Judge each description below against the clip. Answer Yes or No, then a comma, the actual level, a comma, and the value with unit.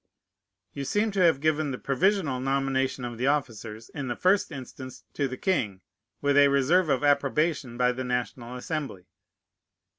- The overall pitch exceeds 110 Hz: Yes, low, 135 Hz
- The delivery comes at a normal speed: Yes, average, 160 wpm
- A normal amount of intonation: Yes, average, 3.4 semitones